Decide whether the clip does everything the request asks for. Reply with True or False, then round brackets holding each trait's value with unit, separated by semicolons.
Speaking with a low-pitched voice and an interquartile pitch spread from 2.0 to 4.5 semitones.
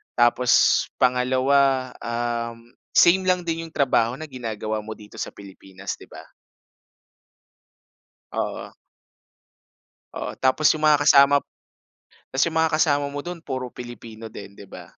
True (130 Hz; 4.0 semitones)